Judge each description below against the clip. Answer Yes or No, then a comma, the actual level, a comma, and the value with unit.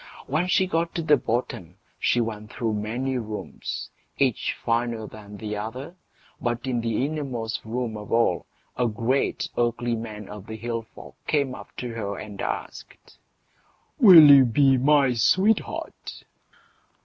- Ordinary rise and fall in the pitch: Yes, average, 3.7 semitones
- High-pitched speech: No, low, 120 Hz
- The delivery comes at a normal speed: Yes, average, 150 wpm